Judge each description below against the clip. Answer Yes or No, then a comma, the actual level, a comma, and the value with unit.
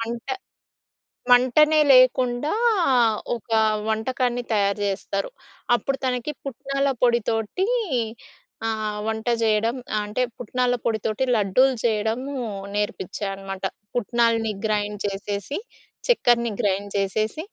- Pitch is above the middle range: Yes, high, 225 Hz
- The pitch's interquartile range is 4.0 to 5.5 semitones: No, average, 3.3 semitones